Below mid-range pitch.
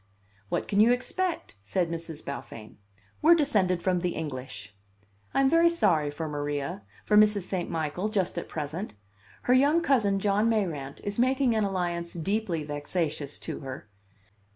No: medium, 185 Hz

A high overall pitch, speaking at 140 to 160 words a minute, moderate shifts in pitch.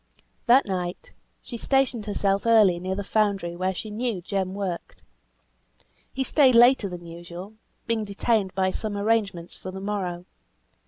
Yes: high, 200 Hz; average, 150 wpm; average, 3.4 semitones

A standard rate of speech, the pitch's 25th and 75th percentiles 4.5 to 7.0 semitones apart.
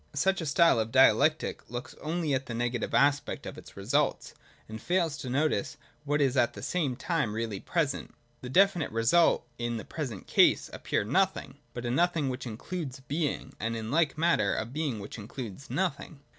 Yes: average, 185 wpm; average, 5.2 semitones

